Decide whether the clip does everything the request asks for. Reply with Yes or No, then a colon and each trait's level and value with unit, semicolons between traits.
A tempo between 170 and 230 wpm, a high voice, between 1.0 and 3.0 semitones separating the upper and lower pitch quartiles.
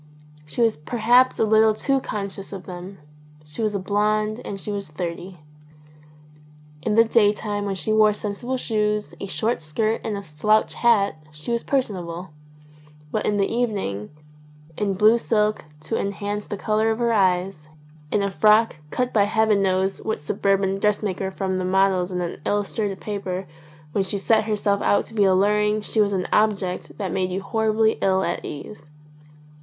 Yes: average, 175 wpm; high, 205 Hz; narrow, 2.4 semitones